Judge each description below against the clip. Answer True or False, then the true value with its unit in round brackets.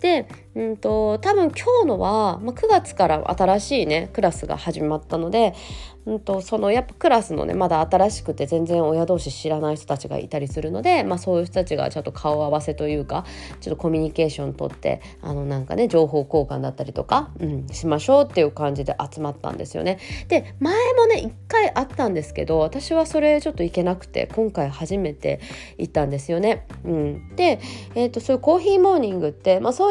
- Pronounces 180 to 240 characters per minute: False (425 characters per minute)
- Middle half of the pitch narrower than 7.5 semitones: False (7.9 semitones)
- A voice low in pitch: False (175 Hz)